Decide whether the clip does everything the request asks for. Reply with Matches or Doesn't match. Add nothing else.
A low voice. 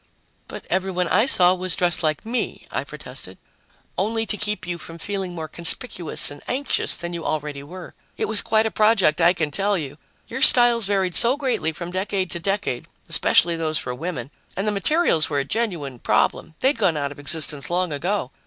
Doesn't match